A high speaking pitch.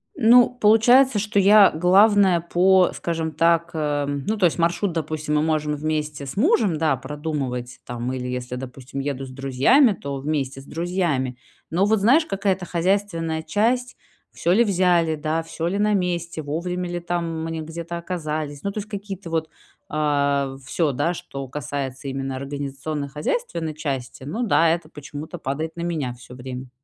No: medium, 160 Hz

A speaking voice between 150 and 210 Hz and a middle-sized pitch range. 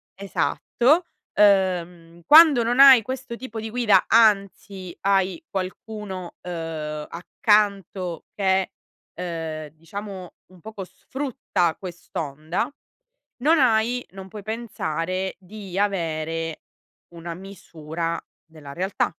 Yes: high, 190 Hz; average, 4.5 semitones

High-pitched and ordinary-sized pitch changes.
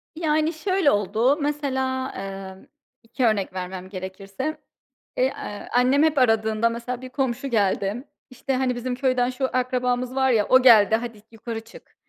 Yes: high, 245 Hz; average, 3.5 semitones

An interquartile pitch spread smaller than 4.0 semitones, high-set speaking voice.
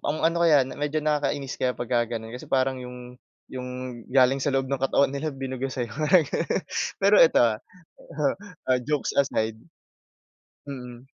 No: average, 2.9 semitones; low, 135 Hz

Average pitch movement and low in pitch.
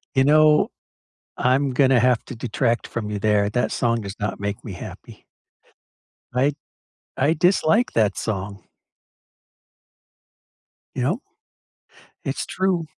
No: wide, 5.7 semitones; low, 125 Hz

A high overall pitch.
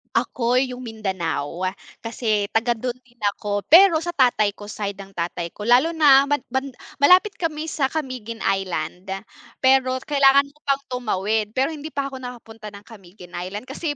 Yes: high, 245 Hz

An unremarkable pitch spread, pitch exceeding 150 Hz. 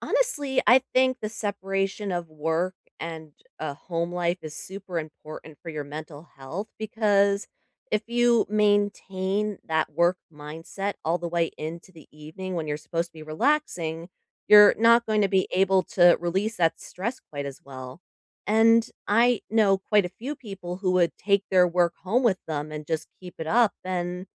Yes: average, 4.4 semitones; medium, 185 Hz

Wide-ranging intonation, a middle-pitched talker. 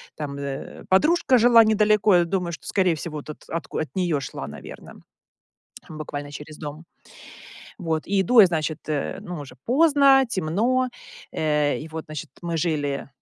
Yes: wide, 5.9 semitones; medium, 165 Hz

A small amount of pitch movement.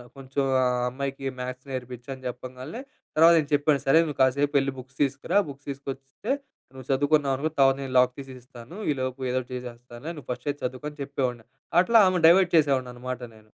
Yes: narrow, 2.2 semitones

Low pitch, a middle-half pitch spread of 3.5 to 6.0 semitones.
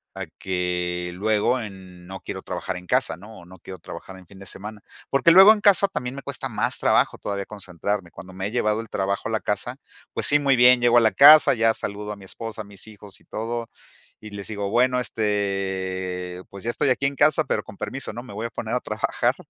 Yes: low, 105 Hz; average, 4.2 semitones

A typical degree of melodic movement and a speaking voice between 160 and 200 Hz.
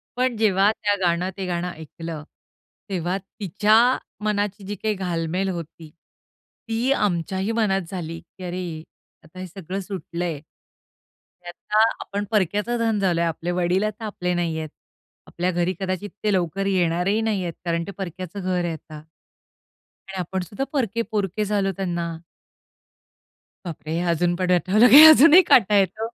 Yes: average, 3.1 semitones; medium, 185 Hz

